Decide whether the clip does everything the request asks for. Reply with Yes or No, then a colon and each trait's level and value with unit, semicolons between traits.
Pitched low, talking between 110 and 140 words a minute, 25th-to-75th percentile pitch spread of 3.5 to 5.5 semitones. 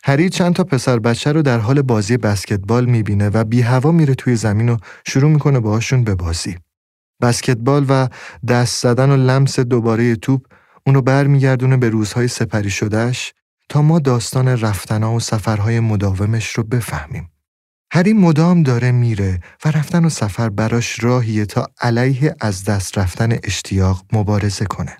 No: low, 120 Hz; fast, 155 wpm; average, 3.8 semitones